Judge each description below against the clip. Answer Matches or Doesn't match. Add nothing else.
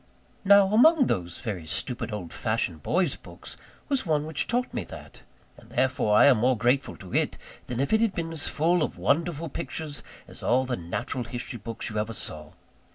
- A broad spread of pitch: Matches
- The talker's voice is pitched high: Doesn't match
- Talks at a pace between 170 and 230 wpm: Matches